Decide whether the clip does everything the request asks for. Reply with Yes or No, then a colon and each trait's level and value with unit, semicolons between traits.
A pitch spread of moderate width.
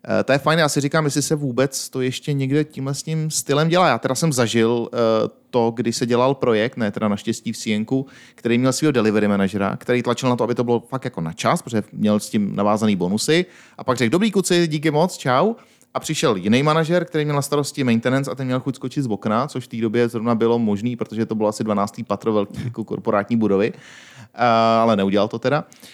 Yes: average, 4.2 semitones